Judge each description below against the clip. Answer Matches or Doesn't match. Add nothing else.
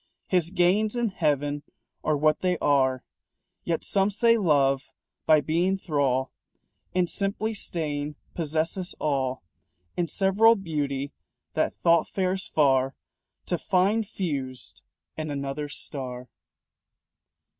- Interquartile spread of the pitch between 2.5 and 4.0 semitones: Doesn't match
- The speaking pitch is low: Doesn't match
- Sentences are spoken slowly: Matches